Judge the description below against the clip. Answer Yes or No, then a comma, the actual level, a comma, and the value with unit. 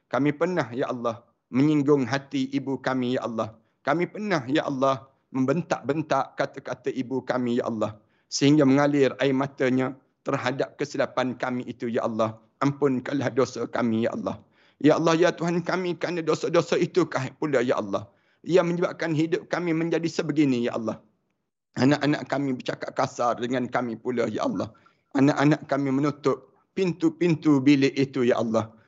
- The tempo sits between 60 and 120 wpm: No, average, 150 wpm